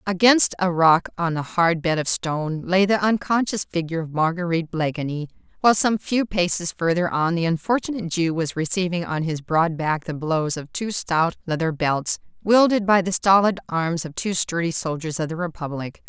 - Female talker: Yes, female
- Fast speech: No, average, 185 wpm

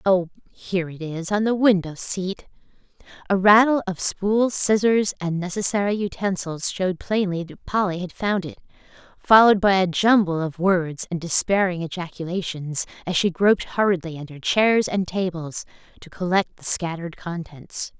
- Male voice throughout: No, female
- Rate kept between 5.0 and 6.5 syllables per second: No, 4.8 syllables/s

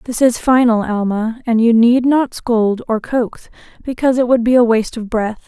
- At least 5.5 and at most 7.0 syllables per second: No, 5.0 syllables/s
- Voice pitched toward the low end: No, high, 235 Hz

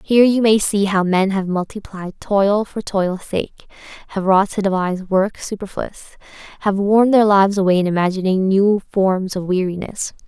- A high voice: Yes, high, 195 Hz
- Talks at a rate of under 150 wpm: No, average, 170 wpm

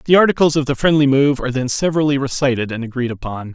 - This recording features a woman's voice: No, male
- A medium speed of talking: No, fast, 220 wpm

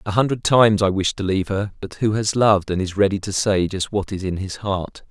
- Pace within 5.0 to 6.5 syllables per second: Yes, 5.7 syllables/s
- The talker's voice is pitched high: No, low, 100 Hz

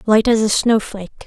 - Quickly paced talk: No, average, 190 wpm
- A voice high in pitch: Yes, high, 215 Hz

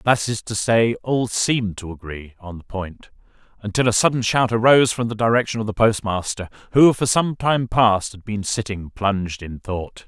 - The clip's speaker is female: No, male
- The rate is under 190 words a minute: No, average, 195 wpm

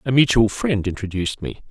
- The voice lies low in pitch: Yes, low, 110 Hz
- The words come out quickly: No, average, 175 wpm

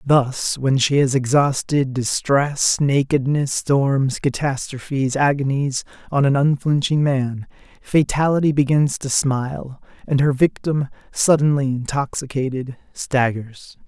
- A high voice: No, low, 135 Hz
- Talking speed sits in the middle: No, slow, 105 wpm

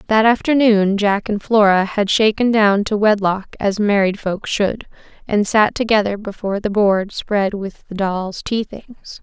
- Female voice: Yes, female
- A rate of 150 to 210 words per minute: Yes, average, 170 wpm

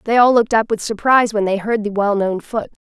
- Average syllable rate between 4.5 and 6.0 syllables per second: No, 6.3 syllables/s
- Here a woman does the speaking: Yes, female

